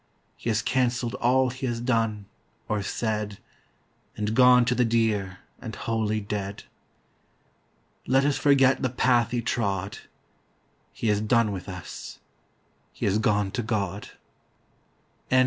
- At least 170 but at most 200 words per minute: No, slow, 135 wpm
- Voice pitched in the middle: No, low, 115 Hz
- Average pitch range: Yes, average, 3.1 semitones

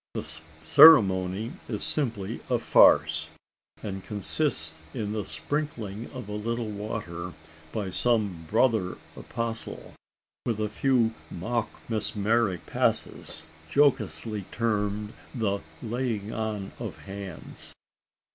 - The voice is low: Yes, low, 105 Hz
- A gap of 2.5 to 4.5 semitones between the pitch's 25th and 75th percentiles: Yes, average, 3.0 semitones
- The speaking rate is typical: No, slow, 105 wpm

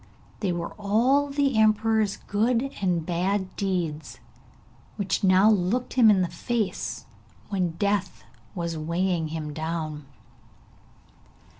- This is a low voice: No, high, 190 Hz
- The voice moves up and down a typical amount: Yes, average, 4.2 semitones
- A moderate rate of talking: No, slow, 115 wpm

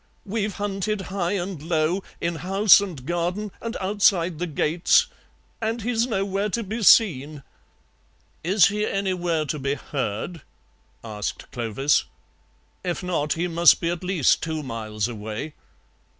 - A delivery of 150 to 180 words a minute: No, slow, 135 wpm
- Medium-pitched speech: Yes, medium, 175 Hz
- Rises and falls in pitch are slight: No, average, 4.7 semitones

